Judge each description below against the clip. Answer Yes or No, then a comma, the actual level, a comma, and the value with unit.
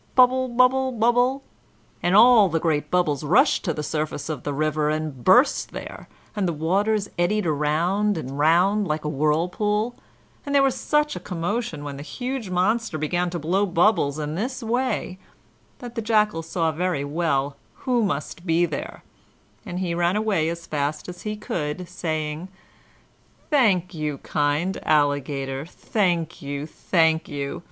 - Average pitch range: No, wide, 5.8 semitones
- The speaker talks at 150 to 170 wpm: Yes, average, 160 wpm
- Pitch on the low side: No, medium, 175 Hz